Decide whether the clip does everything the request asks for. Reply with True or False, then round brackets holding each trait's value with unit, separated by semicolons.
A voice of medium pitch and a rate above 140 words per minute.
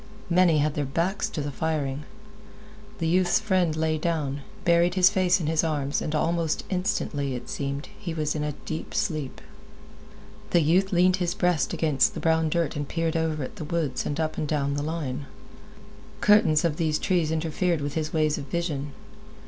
True (160 Hz; 180 wpm)